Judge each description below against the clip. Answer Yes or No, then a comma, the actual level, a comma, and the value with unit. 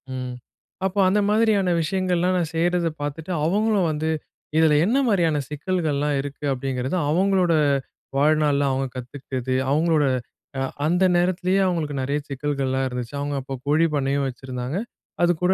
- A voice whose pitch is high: No, medium, 155 Hz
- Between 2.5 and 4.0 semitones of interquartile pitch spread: No, average, 4.5 semitones